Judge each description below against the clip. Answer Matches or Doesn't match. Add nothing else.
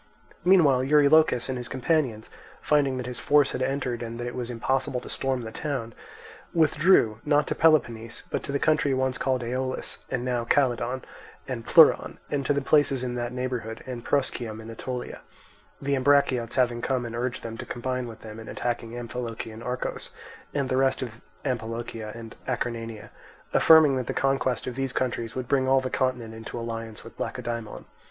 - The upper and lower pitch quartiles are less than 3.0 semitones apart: Matches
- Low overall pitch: Matches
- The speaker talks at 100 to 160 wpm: Doesn't match